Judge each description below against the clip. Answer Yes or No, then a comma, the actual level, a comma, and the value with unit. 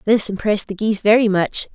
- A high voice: Yes, high, 210 Hz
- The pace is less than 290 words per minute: Yes, fast, 205 wpm